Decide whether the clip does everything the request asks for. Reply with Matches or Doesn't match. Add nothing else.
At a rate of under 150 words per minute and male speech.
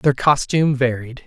Matches